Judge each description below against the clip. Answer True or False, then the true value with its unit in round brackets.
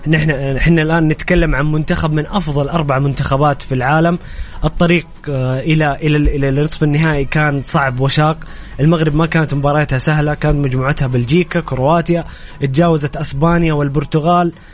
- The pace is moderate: True (125 wpm)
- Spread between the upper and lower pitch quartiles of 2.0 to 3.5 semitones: True (2.8 semitones)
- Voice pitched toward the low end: False (150 Hz)